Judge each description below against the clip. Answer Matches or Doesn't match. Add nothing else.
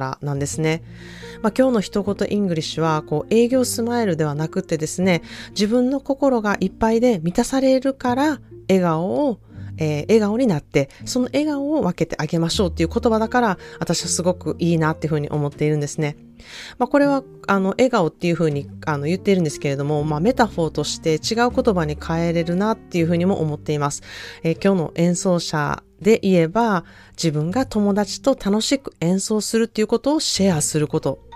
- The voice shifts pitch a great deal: Matches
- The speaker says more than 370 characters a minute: Matches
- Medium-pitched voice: Matches